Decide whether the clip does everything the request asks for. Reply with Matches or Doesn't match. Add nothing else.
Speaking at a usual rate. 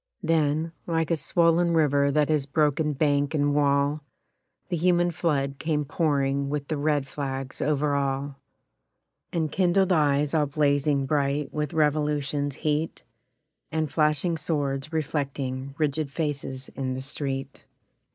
Doesn't match